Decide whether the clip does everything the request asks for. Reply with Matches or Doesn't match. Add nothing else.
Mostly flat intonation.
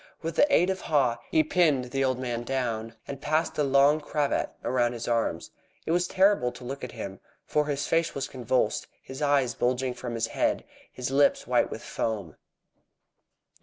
Doesn't match